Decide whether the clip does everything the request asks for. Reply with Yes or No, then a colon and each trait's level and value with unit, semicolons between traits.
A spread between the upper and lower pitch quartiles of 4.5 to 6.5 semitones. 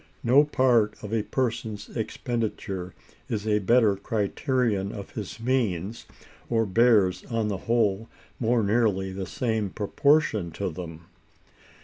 No: average, 3.2 semitones